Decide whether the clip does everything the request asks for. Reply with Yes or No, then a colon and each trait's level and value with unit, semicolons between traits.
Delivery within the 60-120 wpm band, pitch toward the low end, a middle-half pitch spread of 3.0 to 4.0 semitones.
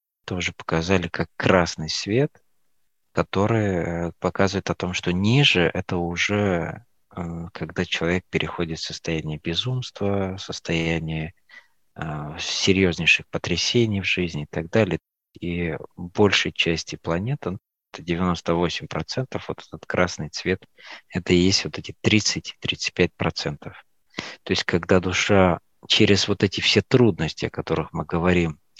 Yes: average, 115 wpm; very low, 90 Hz; average, 3.3 semitones